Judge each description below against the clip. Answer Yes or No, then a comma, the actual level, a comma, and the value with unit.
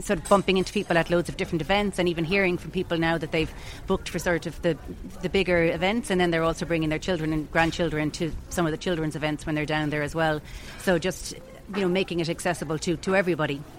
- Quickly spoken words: Yes, fast, 250 wpm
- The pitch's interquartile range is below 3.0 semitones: Yes, narrow, 2.6 semitones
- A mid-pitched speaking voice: Yes, medium, 170 Hz